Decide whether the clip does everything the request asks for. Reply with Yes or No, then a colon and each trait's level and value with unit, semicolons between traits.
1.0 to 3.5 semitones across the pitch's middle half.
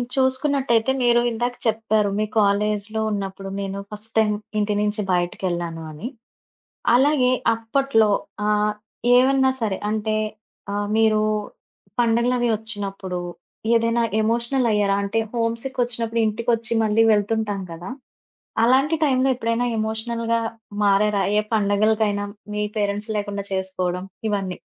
Yes: narrow, 2.5 semitones